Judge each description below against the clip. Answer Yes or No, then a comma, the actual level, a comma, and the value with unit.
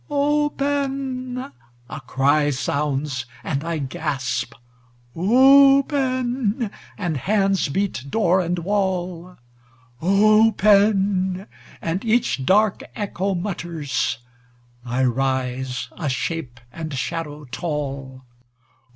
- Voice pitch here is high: No, medium, 175 Hz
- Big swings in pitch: Yes, wide, 7.5 semitones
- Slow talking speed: Yes, slow, 85 wpm